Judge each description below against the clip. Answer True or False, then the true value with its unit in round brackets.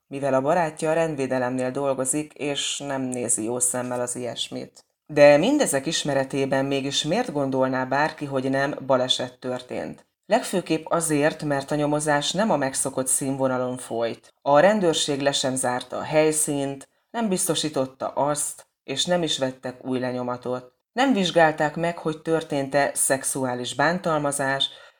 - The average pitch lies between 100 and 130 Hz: False (140 Hz)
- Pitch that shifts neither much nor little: True (3.0 semitones)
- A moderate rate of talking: True (135 wpm)